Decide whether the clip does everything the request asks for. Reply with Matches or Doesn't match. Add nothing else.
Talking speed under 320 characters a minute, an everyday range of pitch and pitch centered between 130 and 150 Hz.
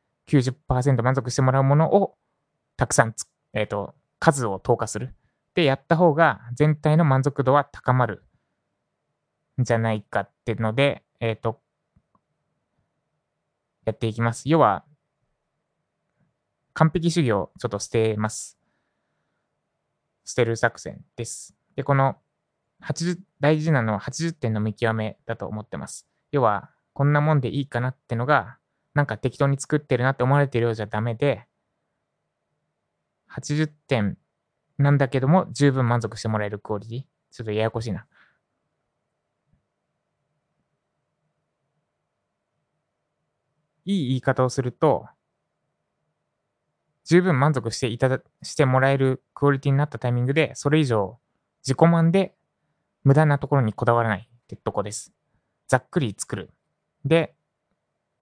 Matches